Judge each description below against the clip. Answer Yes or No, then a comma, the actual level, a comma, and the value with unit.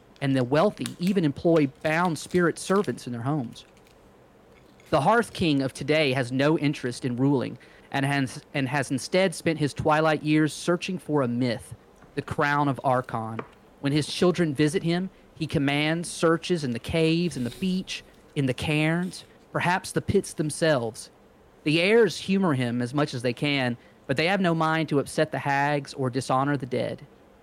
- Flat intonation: No, average, 3.8 semitones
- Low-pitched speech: No, medium, 150 Hz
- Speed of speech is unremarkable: Yes, average, 175 wpm